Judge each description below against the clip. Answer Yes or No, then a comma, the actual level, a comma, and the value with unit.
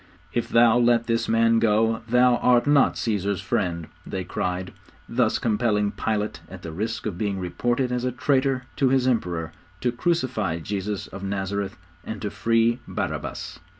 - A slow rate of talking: No, average, 160 wpm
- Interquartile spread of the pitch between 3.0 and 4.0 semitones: Yes, average, 3.4 semitones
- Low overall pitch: Yes, low, 115 Hz